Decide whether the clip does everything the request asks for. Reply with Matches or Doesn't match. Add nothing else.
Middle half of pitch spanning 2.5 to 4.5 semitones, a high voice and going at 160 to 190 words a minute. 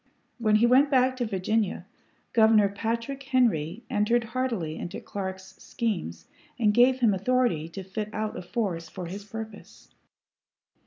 Doesn't match